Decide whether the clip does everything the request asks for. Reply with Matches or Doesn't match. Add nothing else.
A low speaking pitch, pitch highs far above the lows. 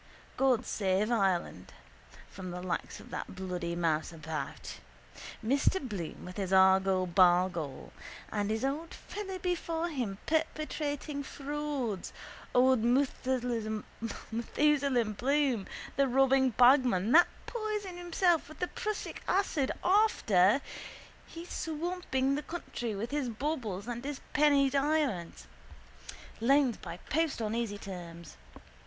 Doesn't match